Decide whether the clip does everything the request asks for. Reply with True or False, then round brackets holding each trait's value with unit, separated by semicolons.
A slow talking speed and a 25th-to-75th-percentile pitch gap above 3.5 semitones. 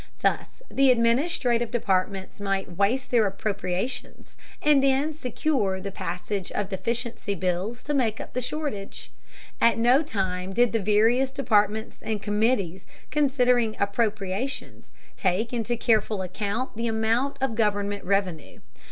True (130 wpm; 4.0 semitones)